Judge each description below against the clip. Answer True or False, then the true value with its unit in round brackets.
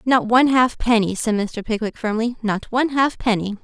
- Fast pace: False (165 wpm)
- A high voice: True (230 Hz)